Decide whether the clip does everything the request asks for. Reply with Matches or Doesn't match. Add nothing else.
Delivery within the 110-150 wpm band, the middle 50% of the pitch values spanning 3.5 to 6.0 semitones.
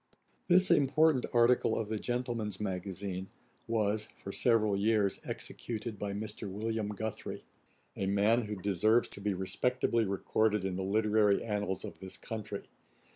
Doesn't match